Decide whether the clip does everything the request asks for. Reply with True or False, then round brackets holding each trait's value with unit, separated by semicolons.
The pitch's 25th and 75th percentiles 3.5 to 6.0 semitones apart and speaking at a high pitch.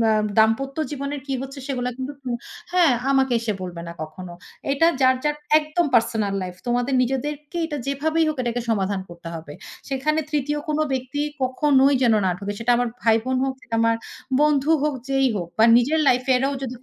True (4.2 semitones; 260 Hz)